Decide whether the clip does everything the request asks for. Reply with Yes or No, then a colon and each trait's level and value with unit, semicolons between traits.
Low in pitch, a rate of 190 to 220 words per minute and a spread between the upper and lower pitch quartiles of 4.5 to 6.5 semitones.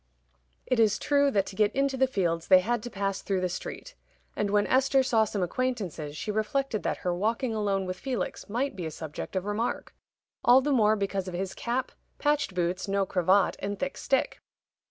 No: high, 210 Hz; average, 200 wpm; average, 5.1 semitones